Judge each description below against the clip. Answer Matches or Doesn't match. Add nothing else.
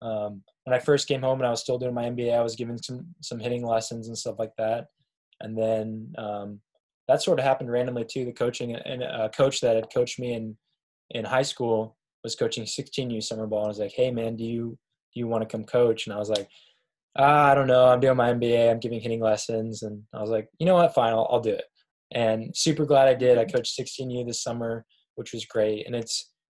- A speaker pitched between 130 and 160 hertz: Doesn't match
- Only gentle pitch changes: Matches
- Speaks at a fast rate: Matches